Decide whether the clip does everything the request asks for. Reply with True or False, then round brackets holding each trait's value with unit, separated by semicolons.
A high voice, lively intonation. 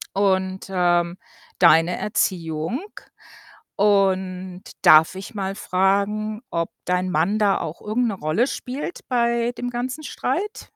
False (195 Hz; 3.2 semitones)